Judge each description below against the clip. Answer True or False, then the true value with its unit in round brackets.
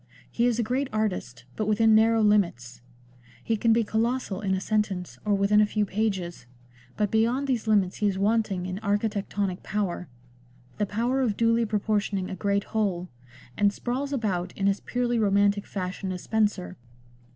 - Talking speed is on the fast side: False (175 wpm)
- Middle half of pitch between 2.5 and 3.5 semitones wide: True (2.8 semitones)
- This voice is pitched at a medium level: False (210 Hz)